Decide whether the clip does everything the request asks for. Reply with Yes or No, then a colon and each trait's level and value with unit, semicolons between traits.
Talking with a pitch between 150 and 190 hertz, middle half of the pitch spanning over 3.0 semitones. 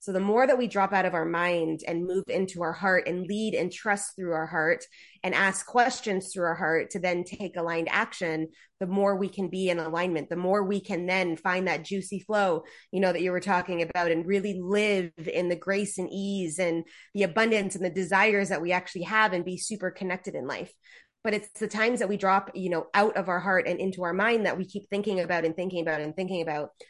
No: medium, 185 Hz; narrow, 2.4 semitones